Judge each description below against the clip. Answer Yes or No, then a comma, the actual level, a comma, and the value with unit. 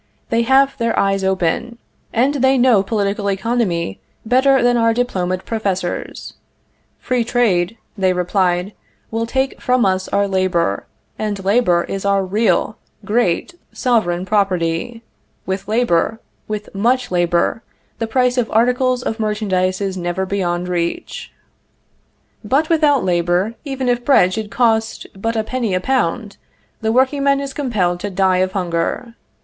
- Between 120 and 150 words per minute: Yes, average, 140 wpm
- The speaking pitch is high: Yes, high, 210 Hz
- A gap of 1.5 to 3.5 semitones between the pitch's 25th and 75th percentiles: No, average, 4.6 semitones